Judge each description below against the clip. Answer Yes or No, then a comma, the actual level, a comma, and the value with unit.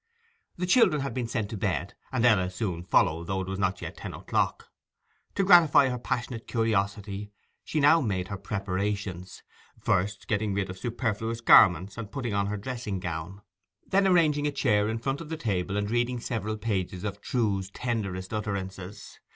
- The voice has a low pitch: Yes, low, 105 Hz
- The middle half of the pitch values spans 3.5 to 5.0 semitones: Yes, average, 4.1 semitones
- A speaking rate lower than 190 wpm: Yes, average, 175 wpm